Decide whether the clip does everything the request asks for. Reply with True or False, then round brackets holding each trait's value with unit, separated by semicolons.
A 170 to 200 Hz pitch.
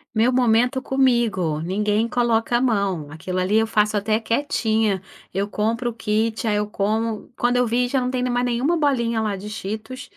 False (225 Hz)